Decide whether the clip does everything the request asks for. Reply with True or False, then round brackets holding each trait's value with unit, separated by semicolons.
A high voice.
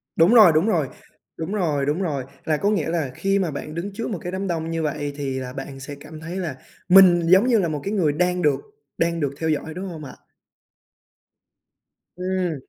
False (165 Hz)